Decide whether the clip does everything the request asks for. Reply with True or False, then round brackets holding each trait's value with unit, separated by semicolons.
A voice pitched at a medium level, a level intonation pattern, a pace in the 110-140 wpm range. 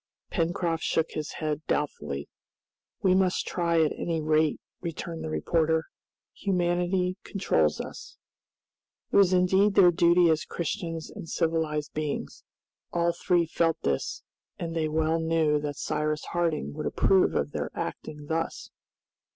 True (165 Hz; 2.3 semitones; 135 wpm)